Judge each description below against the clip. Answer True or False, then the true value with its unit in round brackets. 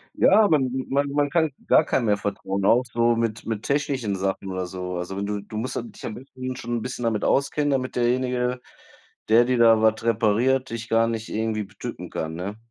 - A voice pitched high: False (115 Hz)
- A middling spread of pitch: True (3.6 semitones)